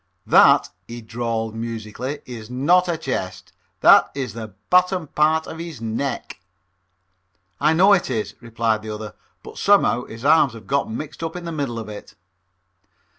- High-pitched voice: No, low, 125 Hz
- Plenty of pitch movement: Yes, wide, 6.0 semitones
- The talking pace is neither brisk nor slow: Yes, average, 165 wpm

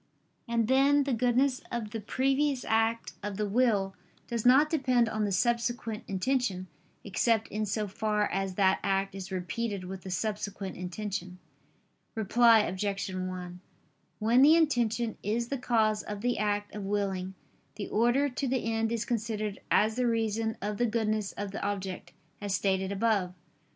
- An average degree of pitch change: Yes, average, 3.3 semitones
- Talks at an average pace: Yes, average, 160 wpm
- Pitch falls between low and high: No, high, 215 Hz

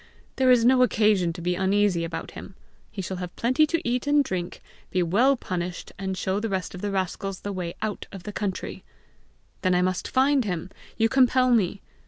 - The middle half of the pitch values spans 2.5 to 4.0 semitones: No, average, 5.0 semitones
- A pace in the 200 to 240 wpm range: Yes, fast, 205 wpm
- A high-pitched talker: Yes, high, 195 Hz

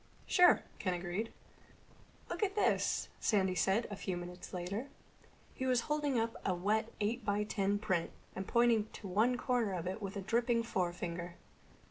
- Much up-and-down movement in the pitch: No, average, 4.2 semitones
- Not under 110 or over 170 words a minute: Yes, average, 165 wpm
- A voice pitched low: No, high, 205 Hz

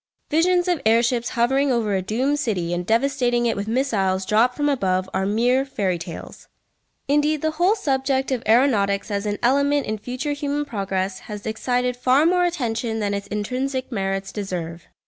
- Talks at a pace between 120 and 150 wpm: No, average, 175 wpm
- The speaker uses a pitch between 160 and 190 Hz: No, high, 240 Hz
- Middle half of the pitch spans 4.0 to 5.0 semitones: No, wide, 5.4 semitones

